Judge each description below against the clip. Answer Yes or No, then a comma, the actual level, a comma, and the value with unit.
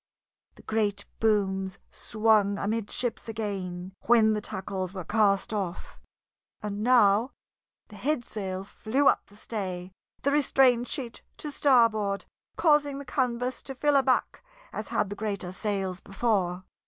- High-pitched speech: Yes, high, 215 Hz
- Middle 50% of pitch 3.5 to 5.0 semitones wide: Yes, average, 3.9 semitones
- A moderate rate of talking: No, slow, 130 wpm